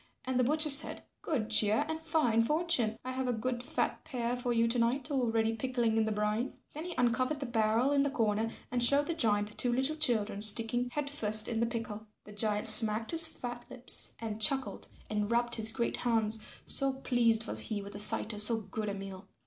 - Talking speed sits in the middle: No, fast, 220 wpm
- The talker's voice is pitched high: Yes, high, 235 Hz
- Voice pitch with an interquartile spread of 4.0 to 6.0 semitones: No, average, 3.2 semitones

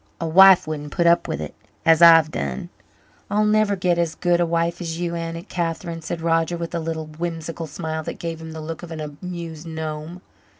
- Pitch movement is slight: Yes, narrow, 1.4 semitones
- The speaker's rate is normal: No, fast, 210 wpm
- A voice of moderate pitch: Yes, medium, 165 Hz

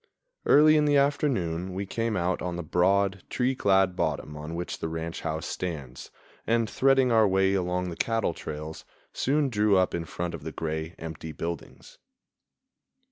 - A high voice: No, very low, 90 Hz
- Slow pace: No, average, 170 wpm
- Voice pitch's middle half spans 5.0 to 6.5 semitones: Yes, wide, 5.5 semitones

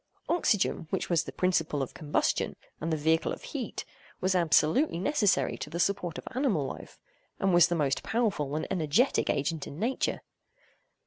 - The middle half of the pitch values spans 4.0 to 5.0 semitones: Yes, average, 4.6 semitones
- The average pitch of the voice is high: No, medium, 175 Hz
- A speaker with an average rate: Yes, average, 170 wpm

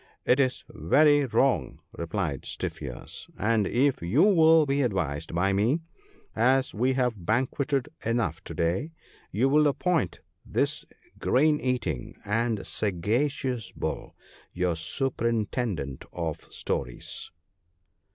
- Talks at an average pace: No, slow, 125 wpm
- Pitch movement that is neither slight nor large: No, wide, 7.0 semitones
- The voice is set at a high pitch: No, low, 115 Hz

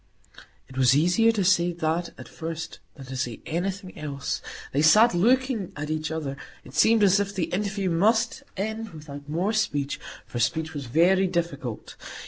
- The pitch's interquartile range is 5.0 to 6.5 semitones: Yes, average, 5.3 semitones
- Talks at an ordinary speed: Yes, average, 170 wpm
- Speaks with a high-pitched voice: No, medium, 170 Hz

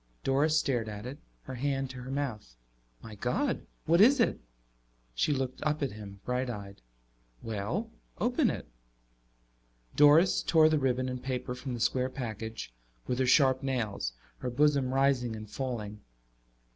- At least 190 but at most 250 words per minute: No, average, 155 wpm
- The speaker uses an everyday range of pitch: Yes, average, 4.1 semitones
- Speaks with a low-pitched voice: Yes, low, 130 Hz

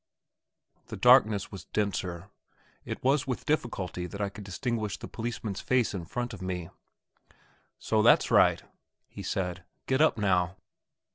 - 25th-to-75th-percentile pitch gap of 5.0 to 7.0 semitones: No, average, 4.6 semitones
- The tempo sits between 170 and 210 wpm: No, average, 145 wpm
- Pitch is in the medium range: No, low, 100 Hz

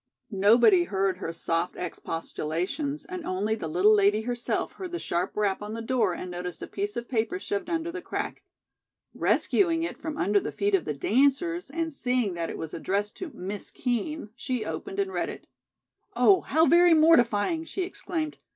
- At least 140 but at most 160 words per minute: No, average, 185 wpm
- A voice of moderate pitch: No, high, 240 Hz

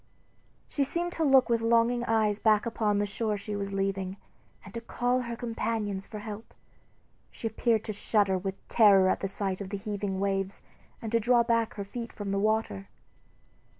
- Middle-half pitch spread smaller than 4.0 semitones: Yes, average, 2.8 semitones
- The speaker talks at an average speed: Yes, average, 190 wpm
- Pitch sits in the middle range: No, high, 215 Hz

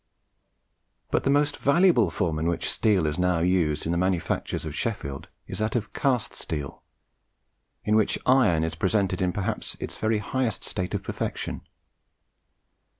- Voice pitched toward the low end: Yes, very low, 95 Hz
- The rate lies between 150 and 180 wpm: Yes, average, 155 wpm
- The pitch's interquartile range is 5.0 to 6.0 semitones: Yes, wide, 5.5 semitones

